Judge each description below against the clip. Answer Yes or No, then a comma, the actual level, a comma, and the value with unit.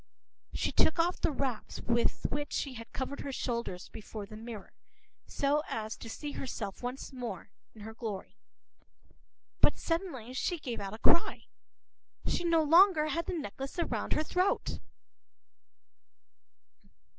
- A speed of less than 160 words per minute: Yes, average, 145 wpm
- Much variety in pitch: Yes, wide, 5.9 semitones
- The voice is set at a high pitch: Yes, very high, 260 Hz